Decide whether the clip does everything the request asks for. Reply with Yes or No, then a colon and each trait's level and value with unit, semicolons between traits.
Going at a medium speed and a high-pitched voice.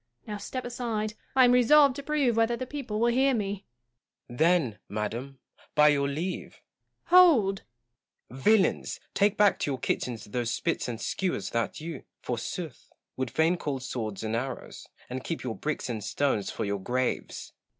No: average, 170 wpm; medium, 160 Hz